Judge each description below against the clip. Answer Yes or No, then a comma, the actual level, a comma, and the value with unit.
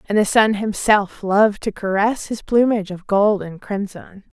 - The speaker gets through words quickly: No, average, 180 wpm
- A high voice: Yes, high, 205 Hz